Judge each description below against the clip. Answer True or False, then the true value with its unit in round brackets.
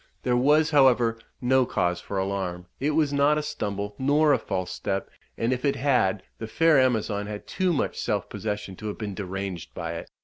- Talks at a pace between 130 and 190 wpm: False (200 wpm)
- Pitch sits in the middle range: False (115 Hz)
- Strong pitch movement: True (6.4 semitones)